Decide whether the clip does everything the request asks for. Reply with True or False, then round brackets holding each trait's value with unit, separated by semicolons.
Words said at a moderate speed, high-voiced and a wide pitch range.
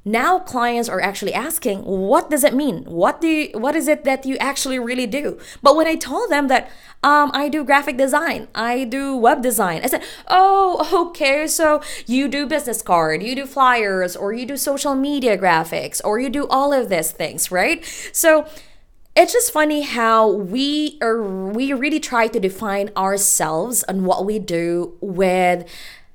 True (180 wpm; 260 Hz; 6.3 semitones)